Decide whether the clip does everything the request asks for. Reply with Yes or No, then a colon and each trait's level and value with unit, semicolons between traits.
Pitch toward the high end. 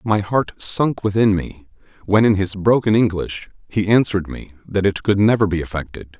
No: low, 100 Hz